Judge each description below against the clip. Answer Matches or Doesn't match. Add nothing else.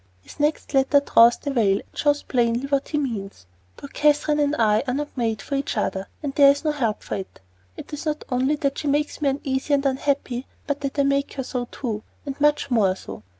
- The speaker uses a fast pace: Matches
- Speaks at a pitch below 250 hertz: Doesn't match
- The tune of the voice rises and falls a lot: Doesn't match